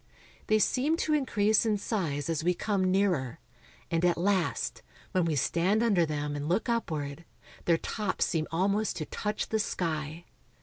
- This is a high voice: No, medium, 180 Hz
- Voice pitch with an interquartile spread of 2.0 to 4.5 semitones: No, average, 5.0 semitones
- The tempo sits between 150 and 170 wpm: Yes, average, 165 wpm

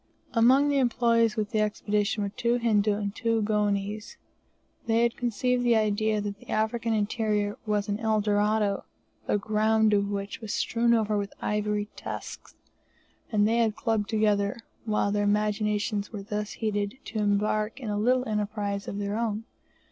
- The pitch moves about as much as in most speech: No, narrow, 1.6 semitones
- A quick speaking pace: No, average, 165 wpm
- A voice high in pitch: Yes, high, 210 Hz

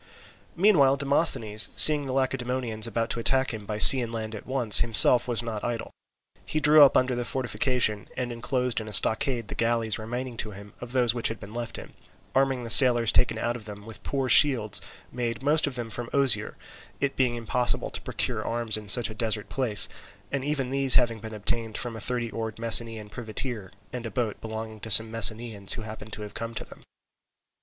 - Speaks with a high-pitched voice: No, low, 115 Hz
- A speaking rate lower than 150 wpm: No, fast, 205 wpm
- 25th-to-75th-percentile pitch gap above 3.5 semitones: No, narrow, 2.6 semitones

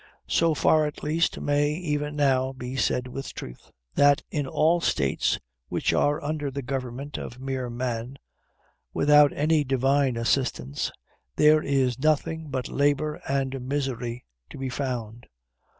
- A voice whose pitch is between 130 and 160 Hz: Yes, low, 135 Hz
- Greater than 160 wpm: No, average, 140 wpm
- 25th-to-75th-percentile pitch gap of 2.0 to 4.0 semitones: Yes, narrow, 2.6 semitones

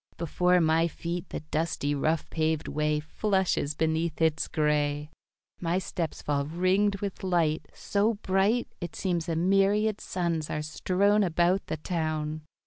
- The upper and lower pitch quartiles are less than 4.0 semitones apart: Yes, average, 3.5 semitones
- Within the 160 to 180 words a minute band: No, average, 140 wpm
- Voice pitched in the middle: Yes, medium, 170 Hz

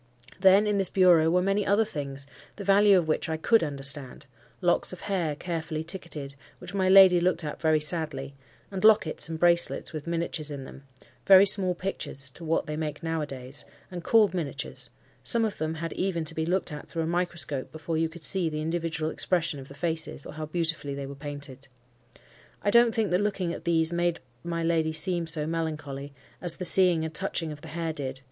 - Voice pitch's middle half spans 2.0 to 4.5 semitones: Yes, average, 3.0 semitones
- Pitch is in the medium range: Yes, medium, 165 Hz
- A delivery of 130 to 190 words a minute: No, fast, 205 wpm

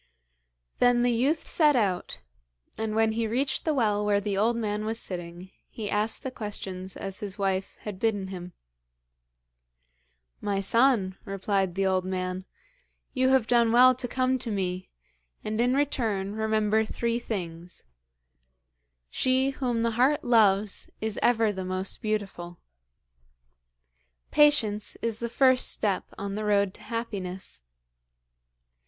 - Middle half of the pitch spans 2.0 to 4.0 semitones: Yes, average, 3.7 semitones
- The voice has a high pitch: Yes, high, 215 Hz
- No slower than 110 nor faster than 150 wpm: Yes, average, 140 wpm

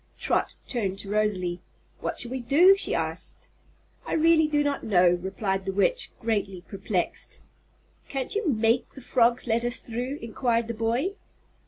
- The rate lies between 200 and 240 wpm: No, average, 160 wpm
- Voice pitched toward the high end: Yes, high, 230 Hz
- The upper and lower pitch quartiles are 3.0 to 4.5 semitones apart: No, average, 5.3 semitones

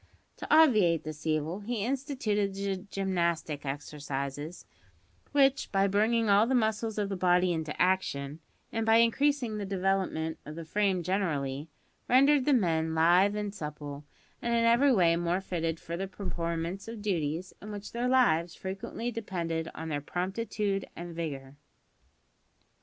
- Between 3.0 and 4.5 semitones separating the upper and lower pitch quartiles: No, average, 5.1 semitones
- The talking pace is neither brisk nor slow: Yes, average, 150 wpm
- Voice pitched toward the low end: No, high, 190 Hz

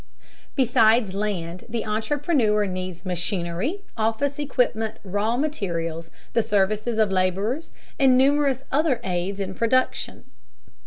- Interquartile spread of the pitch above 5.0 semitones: Yes, wide, 5.5 semitones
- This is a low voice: No, high, 215 Hz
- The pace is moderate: No, slow, 110 wpm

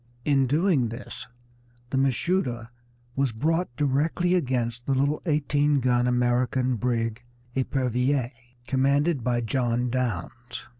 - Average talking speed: No, slow, 115 wpm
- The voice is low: Yes, low, 130 Hz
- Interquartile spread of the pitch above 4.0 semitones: No, average, 2.8 semitones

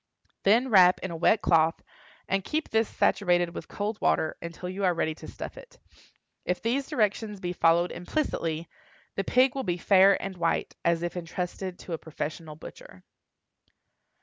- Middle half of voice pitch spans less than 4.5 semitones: Yes, average, 3.9 semitones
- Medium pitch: Yes, medium, 180 Hz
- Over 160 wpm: Yes, average, 170 wpm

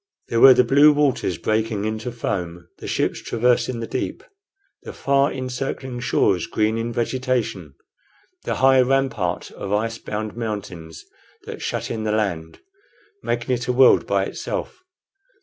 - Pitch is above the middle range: No, low, 115 Hz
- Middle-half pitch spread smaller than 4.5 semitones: Yes, average, 3.5 semitones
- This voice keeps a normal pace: Yes, average, 150 wpm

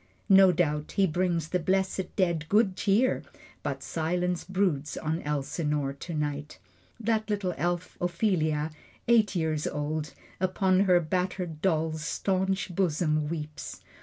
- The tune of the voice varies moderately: Yes, average, 3.6 semitones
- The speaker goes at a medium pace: No, slow, 125 wpm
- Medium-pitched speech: Yes, medium, 175 Hz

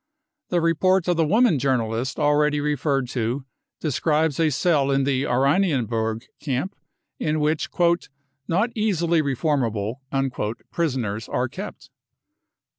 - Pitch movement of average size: Yes, average, 4.7 semitones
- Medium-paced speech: No, slow, 125 wpm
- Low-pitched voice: No, medium, 145 Hz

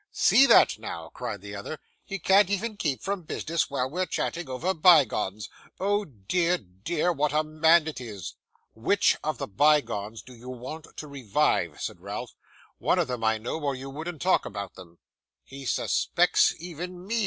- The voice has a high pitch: No, medium, 150 Hz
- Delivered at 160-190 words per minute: Yes, average, 175 wpm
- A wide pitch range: Yes, wide, 6.5 semitones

